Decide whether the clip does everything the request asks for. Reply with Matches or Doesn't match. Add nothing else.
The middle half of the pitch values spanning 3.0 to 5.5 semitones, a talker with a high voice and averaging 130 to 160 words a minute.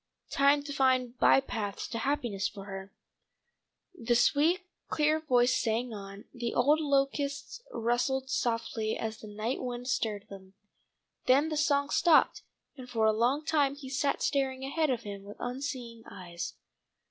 Matches